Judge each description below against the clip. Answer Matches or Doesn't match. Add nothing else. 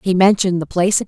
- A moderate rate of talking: Doesn't match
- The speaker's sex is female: Matches